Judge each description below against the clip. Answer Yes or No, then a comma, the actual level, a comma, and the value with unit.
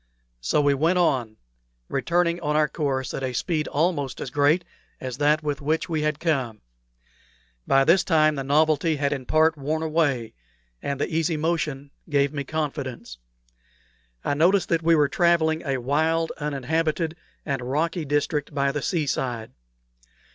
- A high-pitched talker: No, medium, 150 Hz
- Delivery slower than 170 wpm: Yes, average, 160 wpm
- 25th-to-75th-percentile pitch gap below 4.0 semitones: Yes, average, 2.7 semitones